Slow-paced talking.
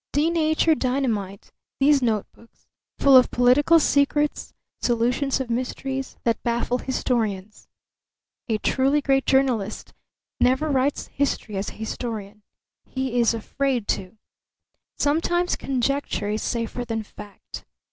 Yes: slow, 115 wpm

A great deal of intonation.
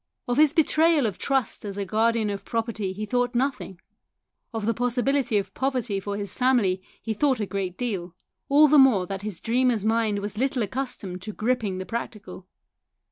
No: average, 4.1 semitones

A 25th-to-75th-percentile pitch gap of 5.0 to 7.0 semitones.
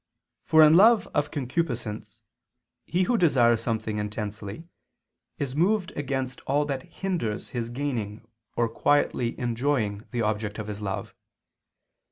Yes: average, 5.3 semitones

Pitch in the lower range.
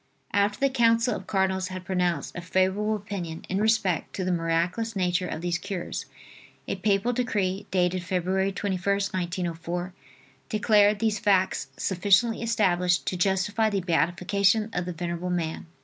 No: high, 190 Hz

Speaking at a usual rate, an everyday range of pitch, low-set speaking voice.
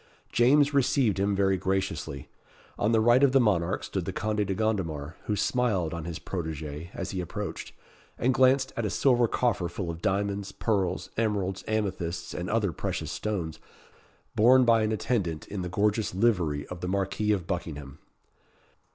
Yes: average, 170 wpm; average, 4.4 semitones; low, 100 Hz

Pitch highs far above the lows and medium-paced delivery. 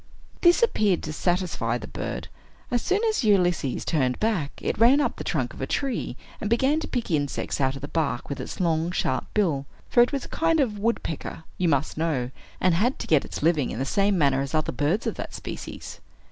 No: wide, 8.3 semitones; fast, 220 wpm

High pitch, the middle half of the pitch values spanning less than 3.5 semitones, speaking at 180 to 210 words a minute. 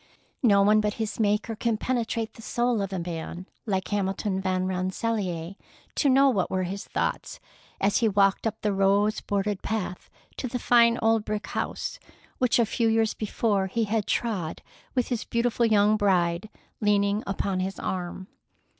No: high, 210 Hz; average, 2.8 semitones; average, 170 wpm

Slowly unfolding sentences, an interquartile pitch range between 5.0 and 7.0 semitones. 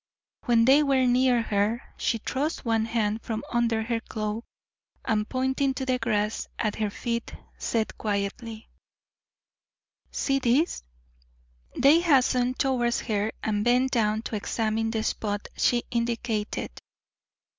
No: slow, 130 wpm; average, 2.7 semitones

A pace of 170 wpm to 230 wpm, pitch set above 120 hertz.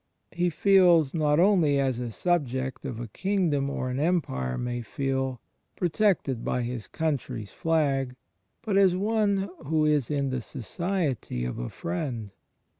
No: average, 155 wpm; medium, 140 Hz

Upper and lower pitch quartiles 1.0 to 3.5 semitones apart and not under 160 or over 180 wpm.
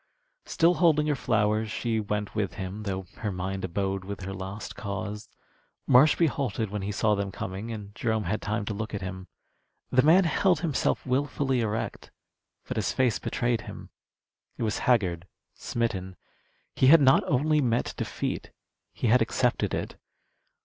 No: average, 4.6 semitones; average, 165 wpm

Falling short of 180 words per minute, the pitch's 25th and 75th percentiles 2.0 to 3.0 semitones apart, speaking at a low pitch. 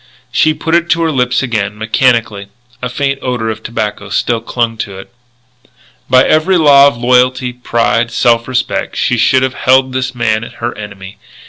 Yes: average, 170 wpm; narrow, 2.5 semitones; low, 125 Hz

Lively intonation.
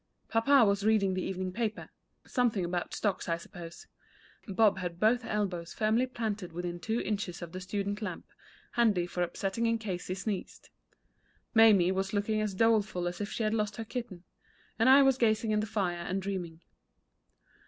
No: average, 3.4 semitones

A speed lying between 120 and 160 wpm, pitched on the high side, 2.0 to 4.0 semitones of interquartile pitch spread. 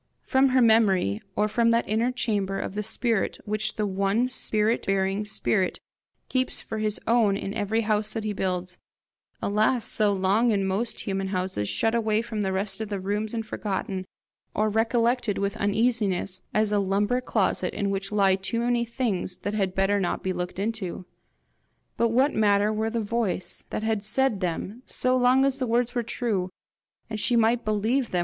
No: average, 185 wpm; high, 215 Hz; average, 3.0 semitones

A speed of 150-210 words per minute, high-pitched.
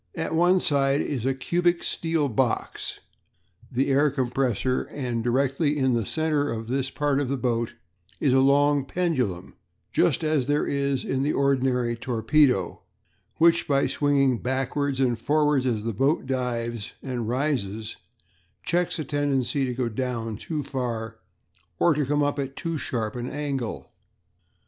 No: average, 155 wpm; low, 135 Hz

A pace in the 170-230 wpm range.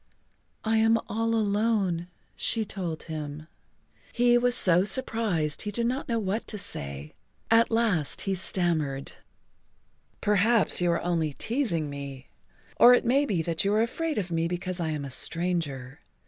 No: average, 155 wpm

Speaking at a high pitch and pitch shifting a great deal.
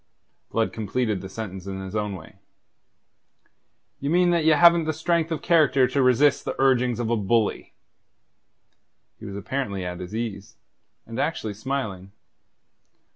No: low, 115 Hz; wide, 6.2 semitones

